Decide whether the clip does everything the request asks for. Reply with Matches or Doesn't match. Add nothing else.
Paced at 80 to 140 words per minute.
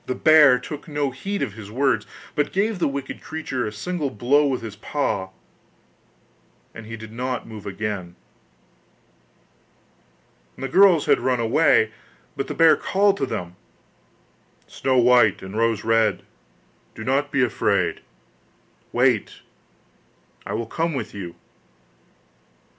Matches